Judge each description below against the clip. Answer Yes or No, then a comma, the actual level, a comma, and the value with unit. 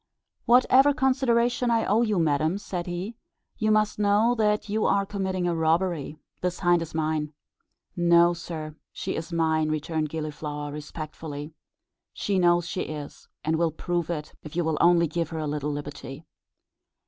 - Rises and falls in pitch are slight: No, average, 4.5 semitones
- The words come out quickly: No, average, 160 wpm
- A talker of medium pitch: Yes, medium, 170 Hz